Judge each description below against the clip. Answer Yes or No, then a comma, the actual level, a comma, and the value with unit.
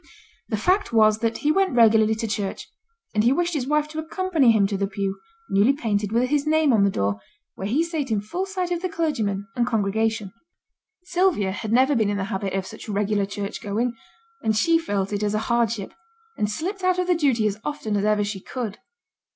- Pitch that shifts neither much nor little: No, wide, 6.8 semitones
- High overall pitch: Yes, high, 225 Hz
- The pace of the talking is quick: Yes, fast, 215 wpm